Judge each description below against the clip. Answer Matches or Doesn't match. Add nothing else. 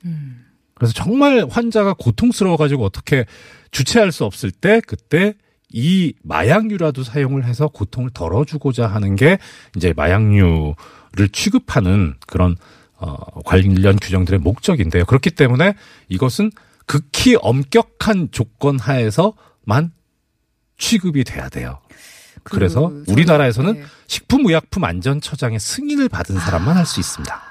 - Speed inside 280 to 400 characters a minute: Matches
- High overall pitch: Doesn't match